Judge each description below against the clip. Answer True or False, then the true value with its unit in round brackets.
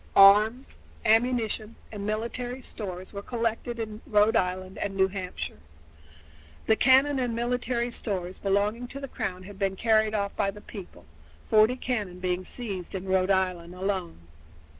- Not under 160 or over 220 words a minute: False (150 wpm)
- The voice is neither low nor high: False (210 Hz)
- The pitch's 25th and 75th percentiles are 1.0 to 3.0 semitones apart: False (3.8 semitones)